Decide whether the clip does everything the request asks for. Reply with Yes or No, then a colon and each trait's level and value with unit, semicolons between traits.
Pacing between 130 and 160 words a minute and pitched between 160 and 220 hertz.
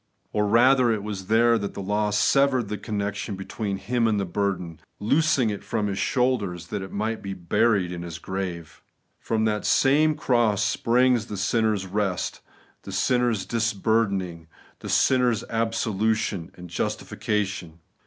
No: average, 155 wpm; low, 105 Hz